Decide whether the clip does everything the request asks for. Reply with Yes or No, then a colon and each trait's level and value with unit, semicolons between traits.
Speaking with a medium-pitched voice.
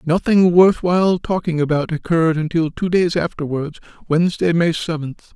Yes: medium, 165 Hz